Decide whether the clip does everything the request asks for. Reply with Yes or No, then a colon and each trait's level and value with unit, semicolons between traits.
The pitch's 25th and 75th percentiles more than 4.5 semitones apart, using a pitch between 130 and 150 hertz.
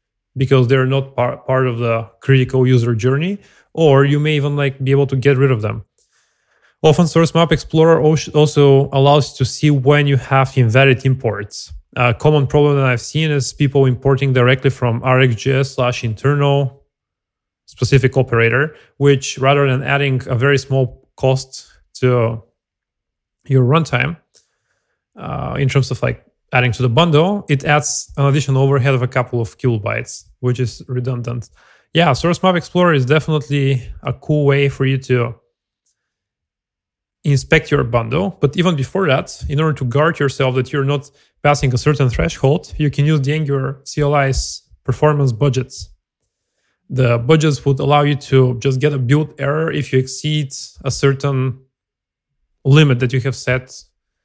No: narrow, 2.4 semitones; low, 135 Hz